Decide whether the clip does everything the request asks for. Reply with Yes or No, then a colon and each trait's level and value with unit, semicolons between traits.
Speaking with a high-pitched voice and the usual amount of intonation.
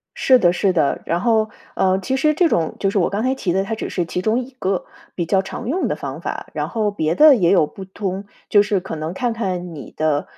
Yes: high, 195 Hz; average, 4.4 semitones